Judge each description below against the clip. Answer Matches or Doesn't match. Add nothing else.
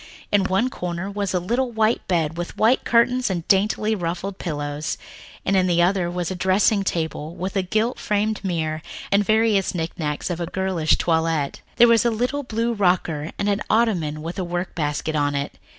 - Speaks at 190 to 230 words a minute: Matches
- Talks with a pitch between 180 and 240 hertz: Matches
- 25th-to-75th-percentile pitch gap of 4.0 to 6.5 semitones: Matches